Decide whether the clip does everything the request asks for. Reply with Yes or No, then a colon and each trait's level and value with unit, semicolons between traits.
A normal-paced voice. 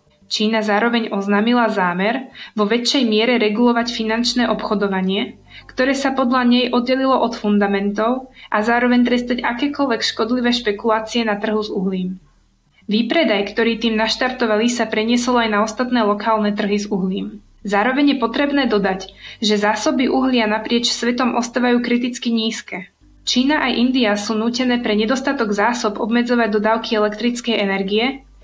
Yes: average, 135 wpm